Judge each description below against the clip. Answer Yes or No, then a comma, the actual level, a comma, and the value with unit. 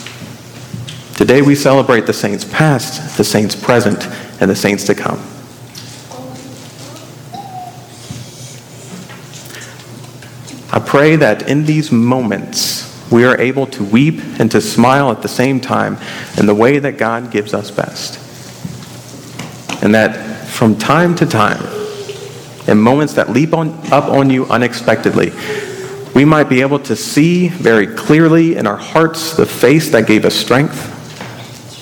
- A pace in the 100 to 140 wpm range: Yes, slow, 135 wpm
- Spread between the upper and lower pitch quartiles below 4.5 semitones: Yes, average, 3.9 semitones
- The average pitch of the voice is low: Yes, low, 130 Hz